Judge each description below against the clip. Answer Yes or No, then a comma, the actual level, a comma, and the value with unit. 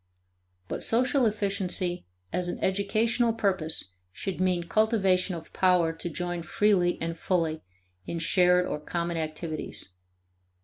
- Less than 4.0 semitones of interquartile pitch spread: Yes, average, 3.1 semitones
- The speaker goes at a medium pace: No, slow, 125 wpm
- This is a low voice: No, medium, 180 Hz